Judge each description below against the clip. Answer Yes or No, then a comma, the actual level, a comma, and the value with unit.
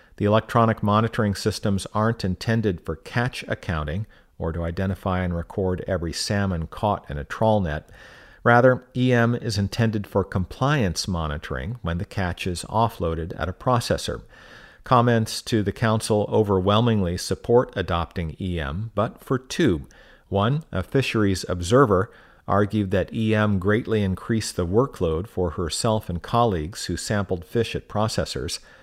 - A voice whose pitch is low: Yes, low, 100 Hz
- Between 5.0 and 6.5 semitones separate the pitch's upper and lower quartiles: No, average, 3.9 semitones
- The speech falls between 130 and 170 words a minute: Yes, average, 140 wpm